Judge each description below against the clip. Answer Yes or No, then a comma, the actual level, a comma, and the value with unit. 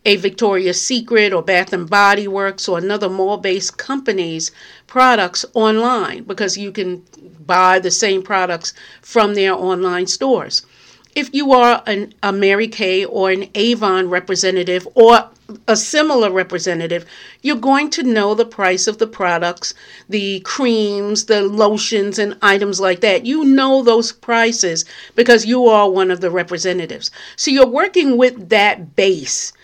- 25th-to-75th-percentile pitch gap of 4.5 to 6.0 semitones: No, average, 3.8 semitones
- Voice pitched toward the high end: Yes, high, 205 Hz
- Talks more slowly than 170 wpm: Yes, average, 150 wpm